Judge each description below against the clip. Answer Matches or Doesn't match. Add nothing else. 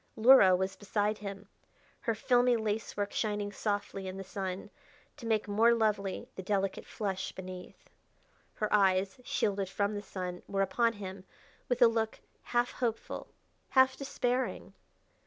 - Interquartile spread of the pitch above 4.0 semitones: Doesn't match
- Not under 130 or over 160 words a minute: Matches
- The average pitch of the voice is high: Matches